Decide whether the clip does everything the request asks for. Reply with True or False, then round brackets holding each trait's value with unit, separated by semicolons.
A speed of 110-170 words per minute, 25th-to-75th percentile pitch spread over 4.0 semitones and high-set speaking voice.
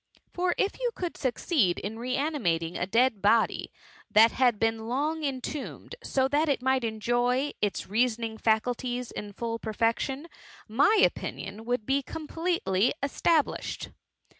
True (140 wpm; 4.4 semitones; 245 Hz)